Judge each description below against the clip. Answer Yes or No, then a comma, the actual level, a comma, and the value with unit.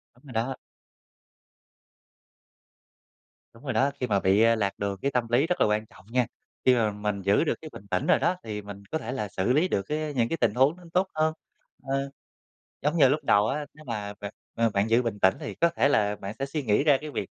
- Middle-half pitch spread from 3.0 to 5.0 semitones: No, wide, 5.6 semitones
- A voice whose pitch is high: No, low, 120 Hz